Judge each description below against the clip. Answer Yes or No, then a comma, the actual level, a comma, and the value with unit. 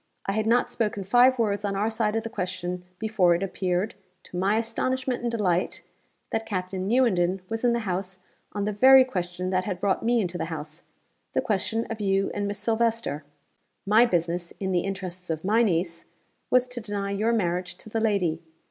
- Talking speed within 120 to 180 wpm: No, average, 195 wpm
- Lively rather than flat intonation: No, average, 3.7 semitones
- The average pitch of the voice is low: No, high, 200 Hz